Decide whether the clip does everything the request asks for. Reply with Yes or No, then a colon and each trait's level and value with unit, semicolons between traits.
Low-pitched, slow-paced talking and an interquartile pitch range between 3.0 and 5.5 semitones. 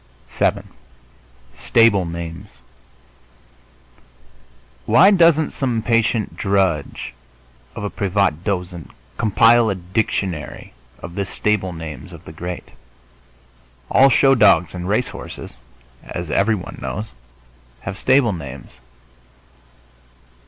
Yes: low, 100 Hz; slow, 100 wpm; average, 4.7 semitones